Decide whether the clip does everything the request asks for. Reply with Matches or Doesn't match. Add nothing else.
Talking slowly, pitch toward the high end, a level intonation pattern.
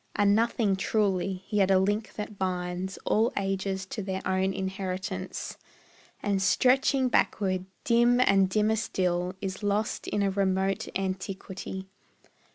Matches